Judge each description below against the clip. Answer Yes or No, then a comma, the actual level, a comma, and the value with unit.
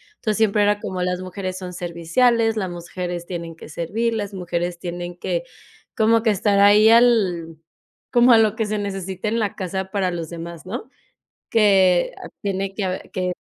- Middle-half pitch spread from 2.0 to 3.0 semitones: No, average, 3.4 semitones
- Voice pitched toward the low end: No, high, 190 Hz